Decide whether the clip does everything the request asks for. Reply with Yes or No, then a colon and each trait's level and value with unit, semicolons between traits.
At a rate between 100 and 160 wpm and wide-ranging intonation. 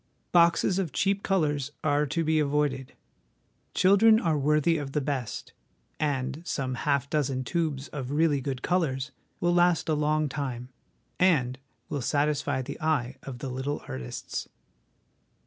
No: average, 145 wpm; average, 3.3 semitones